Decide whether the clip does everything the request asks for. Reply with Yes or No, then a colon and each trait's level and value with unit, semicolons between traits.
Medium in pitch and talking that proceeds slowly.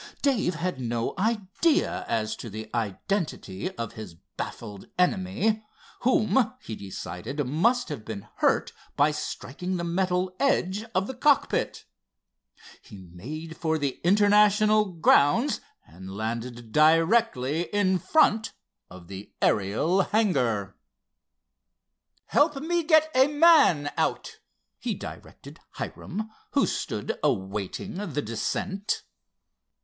Yes: medium, 175 Hz; slow, 115 wpm